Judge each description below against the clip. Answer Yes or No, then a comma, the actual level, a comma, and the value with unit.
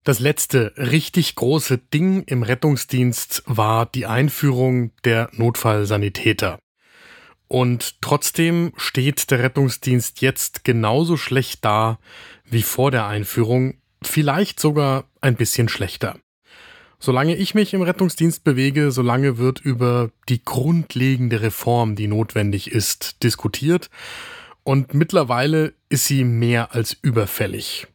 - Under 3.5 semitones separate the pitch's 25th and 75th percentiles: No, average, 4.1 semitones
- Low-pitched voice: Yes, low, 130 Hz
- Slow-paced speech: Yes, slow, 115 wpm